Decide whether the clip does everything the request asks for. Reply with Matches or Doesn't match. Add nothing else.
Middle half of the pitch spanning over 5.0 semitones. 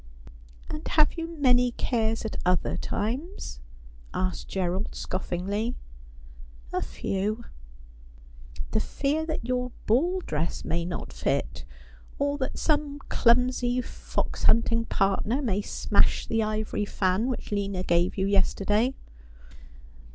Matches